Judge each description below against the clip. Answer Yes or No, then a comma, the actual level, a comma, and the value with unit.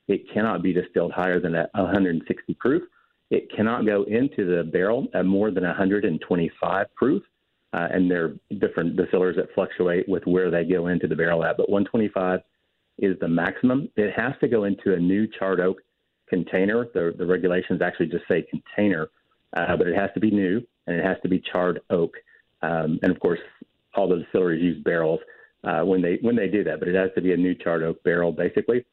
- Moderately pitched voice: No, very low, 90 Hz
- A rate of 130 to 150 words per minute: No, fast, 205 wpm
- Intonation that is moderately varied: No, narrow, 2.1 semitones